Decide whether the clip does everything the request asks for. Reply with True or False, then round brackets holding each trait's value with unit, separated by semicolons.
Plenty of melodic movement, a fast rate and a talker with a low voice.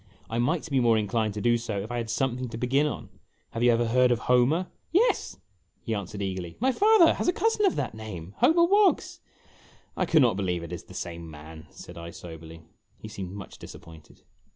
True (6.6 semitones; 225 wpm; 115 Hz)